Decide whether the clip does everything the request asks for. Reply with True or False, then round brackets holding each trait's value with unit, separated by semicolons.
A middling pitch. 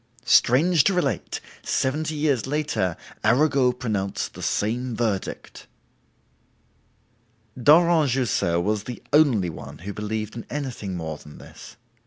False (120 Hz)